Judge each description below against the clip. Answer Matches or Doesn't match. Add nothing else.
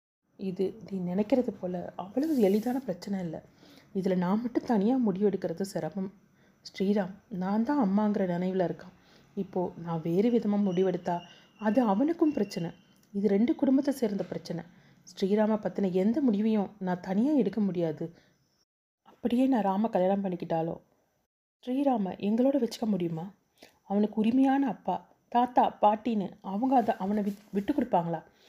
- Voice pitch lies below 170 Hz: Doesn't match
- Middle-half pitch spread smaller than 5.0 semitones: Matches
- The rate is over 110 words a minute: Matches